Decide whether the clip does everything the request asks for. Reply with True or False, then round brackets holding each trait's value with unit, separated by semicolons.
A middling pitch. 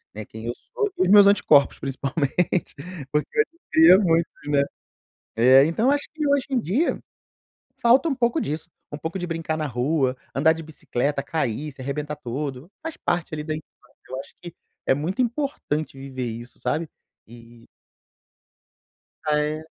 True (155 Hz)